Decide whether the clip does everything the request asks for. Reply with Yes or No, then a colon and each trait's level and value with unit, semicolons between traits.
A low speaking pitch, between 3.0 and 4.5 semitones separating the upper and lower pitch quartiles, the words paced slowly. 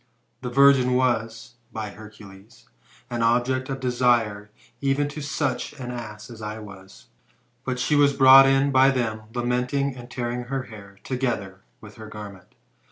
No: low, 120 Hz; average, 3.5 semitones; average, 155 wpm